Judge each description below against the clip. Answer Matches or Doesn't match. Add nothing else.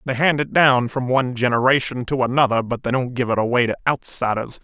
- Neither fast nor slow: Doesn't match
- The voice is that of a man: Matches